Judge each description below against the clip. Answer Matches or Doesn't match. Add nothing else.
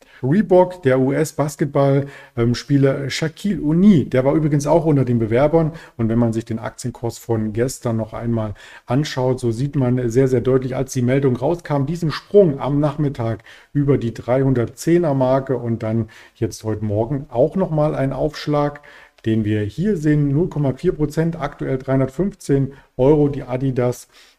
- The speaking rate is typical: Matches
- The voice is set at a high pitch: Doesn't match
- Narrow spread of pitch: Doesn't match